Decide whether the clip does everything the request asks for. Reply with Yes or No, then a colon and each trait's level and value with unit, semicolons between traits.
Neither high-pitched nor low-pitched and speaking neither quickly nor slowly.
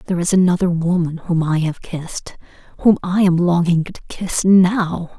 Yes: medium, 175 Hz; average, 160 wpm